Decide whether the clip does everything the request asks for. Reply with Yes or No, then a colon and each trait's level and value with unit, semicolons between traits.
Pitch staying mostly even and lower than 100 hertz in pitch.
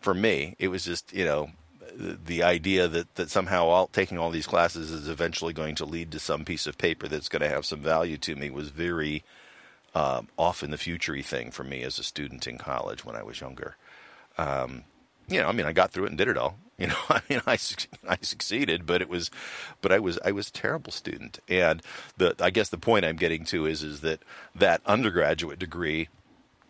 Yes: narrow, 2.1 semitones; very low, 80 Hz